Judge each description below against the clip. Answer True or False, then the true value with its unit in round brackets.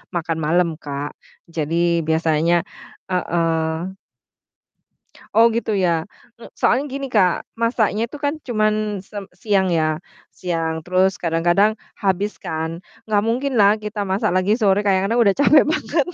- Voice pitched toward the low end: False (190 Hz)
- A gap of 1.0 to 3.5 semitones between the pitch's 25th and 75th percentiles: False (4.5 semitones)